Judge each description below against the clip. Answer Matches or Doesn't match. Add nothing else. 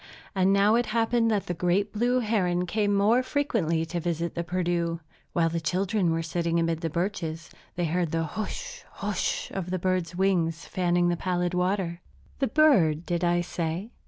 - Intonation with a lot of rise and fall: Doesn't match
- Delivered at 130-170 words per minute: Doesn't match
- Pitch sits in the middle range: Matches